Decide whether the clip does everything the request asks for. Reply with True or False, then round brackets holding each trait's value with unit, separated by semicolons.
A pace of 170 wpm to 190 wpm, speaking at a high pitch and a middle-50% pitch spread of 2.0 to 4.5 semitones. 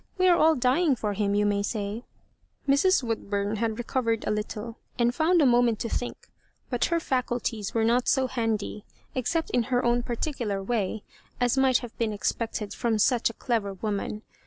True (185 wpm; 235 Hz; 3.2 semitones)